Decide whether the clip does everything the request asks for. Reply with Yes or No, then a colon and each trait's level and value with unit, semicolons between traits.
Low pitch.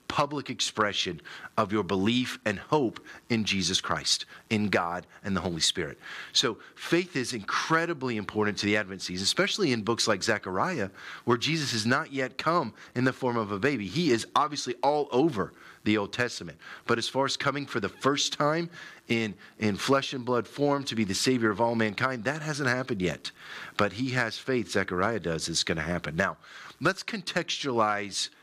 Yes: low, 120 Hz